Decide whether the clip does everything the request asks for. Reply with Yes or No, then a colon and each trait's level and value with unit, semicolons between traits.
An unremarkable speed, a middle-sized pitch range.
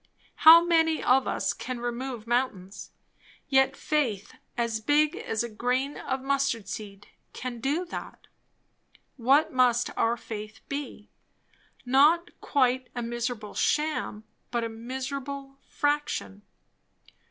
No: slow, 120 wpm; average, 3.4 semitones